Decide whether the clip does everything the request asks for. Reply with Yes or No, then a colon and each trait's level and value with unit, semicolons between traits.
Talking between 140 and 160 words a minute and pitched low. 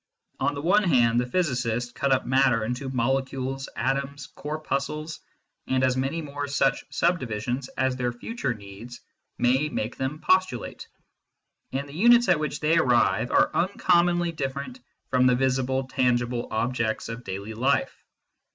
Yes: average, 150 wpm; low, 130 Hz